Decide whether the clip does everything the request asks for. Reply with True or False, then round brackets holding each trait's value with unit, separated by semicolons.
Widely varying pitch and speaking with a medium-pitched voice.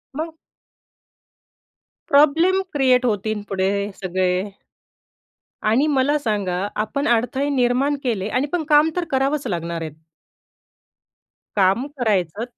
False (6.2 semitones; 250 Hz)